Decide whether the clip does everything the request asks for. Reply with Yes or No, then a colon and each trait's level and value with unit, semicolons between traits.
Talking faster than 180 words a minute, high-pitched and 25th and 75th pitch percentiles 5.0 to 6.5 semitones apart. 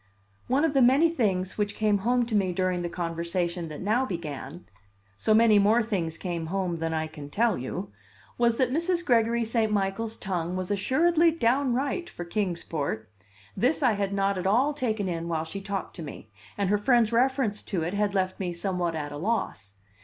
Yes: average, 200 wpm; high, 200 Hz; wide, 5.4 semitones